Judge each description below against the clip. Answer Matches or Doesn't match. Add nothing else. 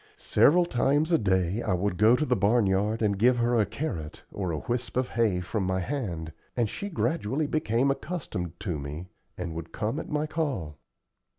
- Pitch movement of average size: Doesn't match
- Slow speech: Doesn't match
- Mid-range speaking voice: Doesn't match